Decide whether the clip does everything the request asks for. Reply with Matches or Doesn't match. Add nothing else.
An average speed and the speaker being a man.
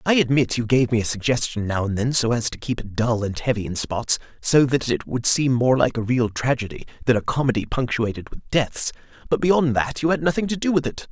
Doesn't match